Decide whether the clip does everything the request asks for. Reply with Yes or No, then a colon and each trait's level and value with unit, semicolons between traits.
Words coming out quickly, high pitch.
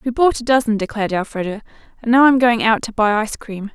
Yes: fast, 240 wpm; high, 230 Hz